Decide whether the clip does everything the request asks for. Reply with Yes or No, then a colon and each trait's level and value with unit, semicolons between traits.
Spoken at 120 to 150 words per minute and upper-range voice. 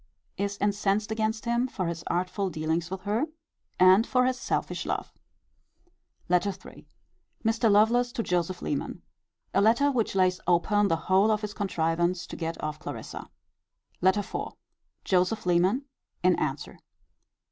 Yes: average, 145 wpm; high, 200 Hz